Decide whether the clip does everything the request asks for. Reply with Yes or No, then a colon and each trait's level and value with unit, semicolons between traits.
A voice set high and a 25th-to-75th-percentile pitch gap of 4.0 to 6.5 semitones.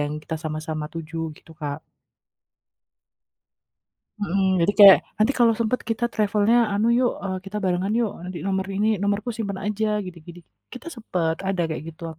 Yes: high, 195 Hz; average, 4.3 semitones